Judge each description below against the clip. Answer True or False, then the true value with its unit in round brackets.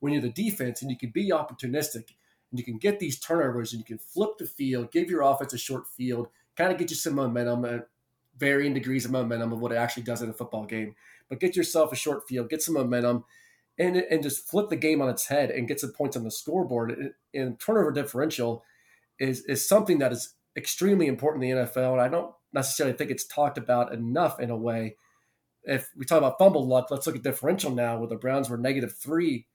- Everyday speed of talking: False (230 wpm)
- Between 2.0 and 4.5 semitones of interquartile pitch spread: True (4.1 semitones)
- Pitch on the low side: True (130 Hz)